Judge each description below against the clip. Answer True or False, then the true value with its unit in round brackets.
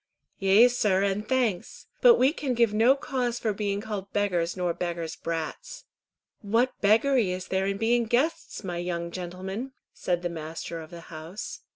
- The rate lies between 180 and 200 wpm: False (170 wpm)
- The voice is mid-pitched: False (200 Hz)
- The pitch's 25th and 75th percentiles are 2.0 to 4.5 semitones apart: False (5.4 semitones)